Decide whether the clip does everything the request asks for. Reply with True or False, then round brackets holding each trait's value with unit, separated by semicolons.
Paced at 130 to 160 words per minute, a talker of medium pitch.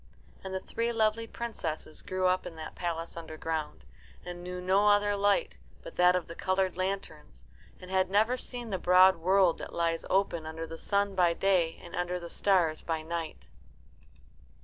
False (175 wpm; 180 Hz)